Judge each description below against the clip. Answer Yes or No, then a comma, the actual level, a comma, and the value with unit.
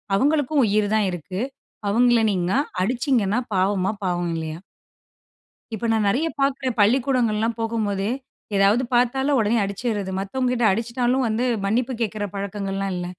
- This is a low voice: No, high, 220 Hz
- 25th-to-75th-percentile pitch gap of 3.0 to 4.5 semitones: Yes, average, 3.9 semitones